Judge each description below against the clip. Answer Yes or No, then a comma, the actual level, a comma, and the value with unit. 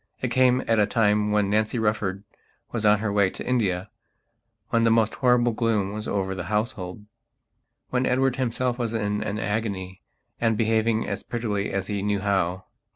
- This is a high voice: No, low, 105 Hz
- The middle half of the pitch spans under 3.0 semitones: Yes, narrow, 2.4 semitones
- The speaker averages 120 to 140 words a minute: No, average, 175 wpm